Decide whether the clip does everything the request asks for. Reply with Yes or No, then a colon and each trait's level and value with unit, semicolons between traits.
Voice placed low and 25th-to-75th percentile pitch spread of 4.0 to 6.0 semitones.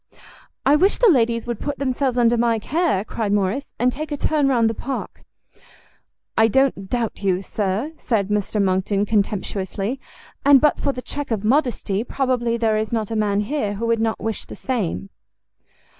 No: high, 230 Hz; average, 4.4 semitones